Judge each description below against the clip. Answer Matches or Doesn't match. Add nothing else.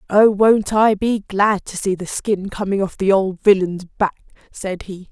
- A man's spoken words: Doesn't match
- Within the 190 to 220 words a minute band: Matches